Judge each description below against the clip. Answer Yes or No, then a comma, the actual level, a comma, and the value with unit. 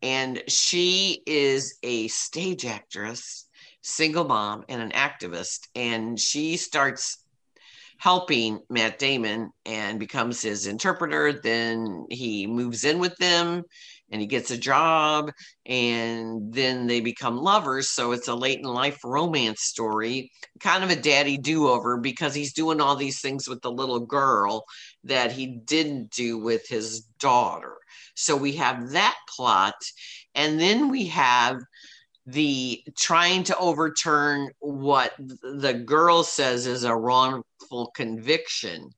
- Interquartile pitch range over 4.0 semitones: Yes, average, 4.4 semitones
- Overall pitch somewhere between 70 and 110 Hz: No, low, 130 Hz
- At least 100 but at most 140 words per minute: Yes, slow, 135 wpm